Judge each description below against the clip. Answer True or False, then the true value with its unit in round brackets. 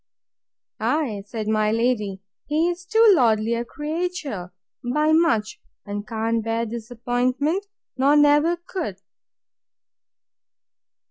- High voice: True (245 Hz)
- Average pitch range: False (6.2 semitones)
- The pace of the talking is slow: True (105 wpm)